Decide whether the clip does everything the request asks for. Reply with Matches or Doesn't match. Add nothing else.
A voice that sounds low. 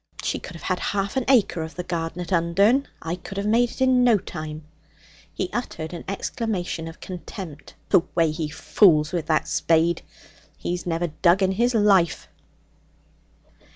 Doesn't match